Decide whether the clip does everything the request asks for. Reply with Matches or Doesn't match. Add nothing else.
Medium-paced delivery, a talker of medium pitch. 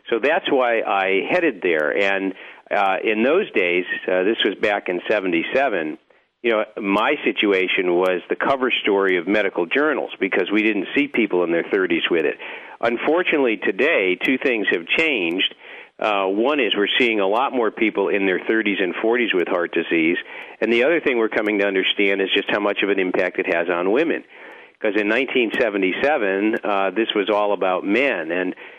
Doesn't match